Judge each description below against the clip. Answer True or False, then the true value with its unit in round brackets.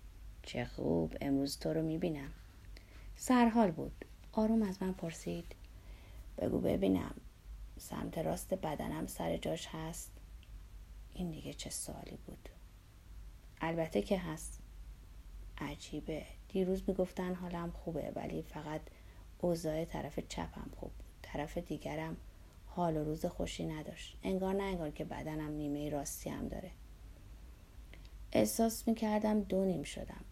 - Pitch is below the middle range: False (145 Hz)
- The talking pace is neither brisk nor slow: True (120 wpm)